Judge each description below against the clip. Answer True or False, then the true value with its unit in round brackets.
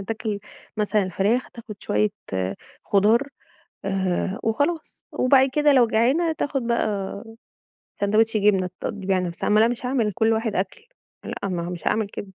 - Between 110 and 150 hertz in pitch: False (215 Hz)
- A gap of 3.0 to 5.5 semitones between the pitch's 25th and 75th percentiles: True (3.6 semitones)